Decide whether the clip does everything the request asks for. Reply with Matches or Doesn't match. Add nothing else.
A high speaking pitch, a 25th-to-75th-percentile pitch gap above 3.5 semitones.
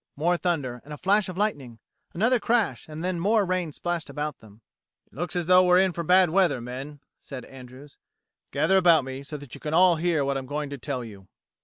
Doesn't match